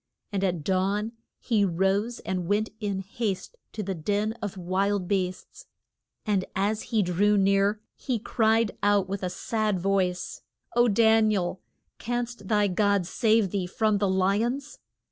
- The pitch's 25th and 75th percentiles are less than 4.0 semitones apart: Yes, narrow, 2.4 semitones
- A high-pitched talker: Yes, high, 200 Hz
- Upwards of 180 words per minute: No, average, 160 wpm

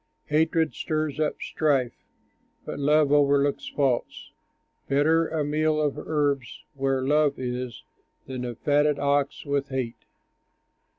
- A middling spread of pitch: No, narrow, 2.1 semitones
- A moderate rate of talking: No, slow, 120 wpm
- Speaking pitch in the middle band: Yes, medium, 145 Hz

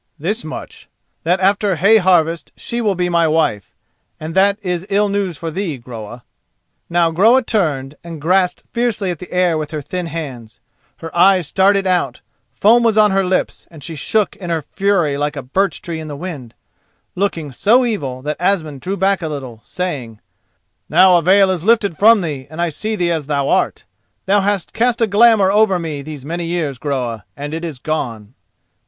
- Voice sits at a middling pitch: Yes, medium, 170 Hz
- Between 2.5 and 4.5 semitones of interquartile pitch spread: No, average, 4.9 semitones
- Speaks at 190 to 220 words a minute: Yes, average, 195 wpm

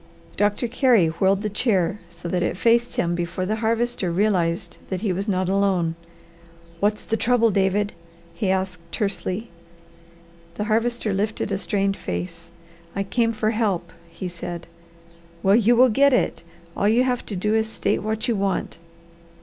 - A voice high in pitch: Yes, high, 200 Hz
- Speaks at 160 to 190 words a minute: Yes, average, 165 wpm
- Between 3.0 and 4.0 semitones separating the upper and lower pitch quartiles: Yes, average, 3.4 semitones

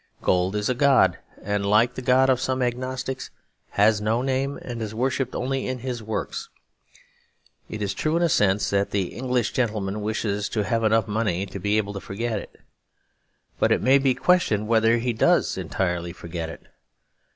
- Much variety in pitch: No, average, 4.0 semitones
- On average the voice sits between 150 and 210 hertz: No, low, 110 Hz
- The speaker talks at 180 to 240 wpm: Yes, average, 185 wpm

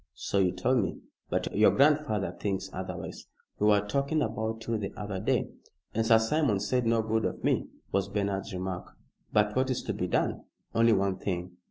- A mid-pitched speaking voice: No, low, 105 Hz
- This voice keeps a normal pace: Yes, average, 190 wpm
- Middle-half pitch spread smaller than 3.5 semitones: Yes, average, 2.9 semitones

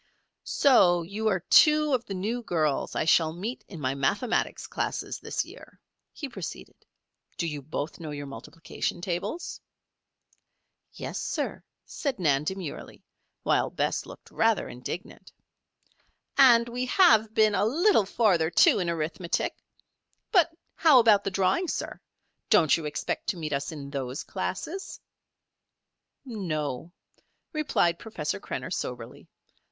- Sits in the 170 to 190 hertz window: Yes, medium, 185 Hz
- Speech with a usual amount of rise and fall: No, wide, 7.0 semitones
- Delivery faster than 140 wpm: No, slow, 135 wpm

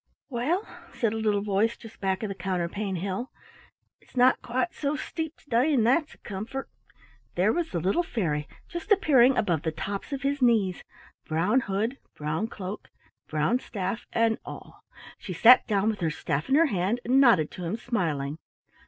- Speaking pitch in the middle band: No, high, 215 Hz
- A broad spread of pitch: Yes, wide, 5.7 semitones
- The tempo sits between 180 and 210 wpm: Yes, average, 185 wpm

